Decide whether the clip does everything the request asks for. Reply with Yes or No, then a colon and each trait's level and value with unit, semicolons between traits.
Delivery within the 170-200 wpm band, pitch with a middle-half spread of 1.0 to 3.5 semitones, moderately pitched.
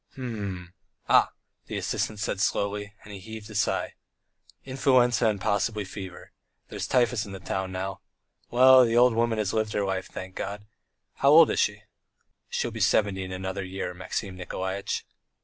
No: average, 175 wpm; average, 3.2 semitones; low, 105 Hz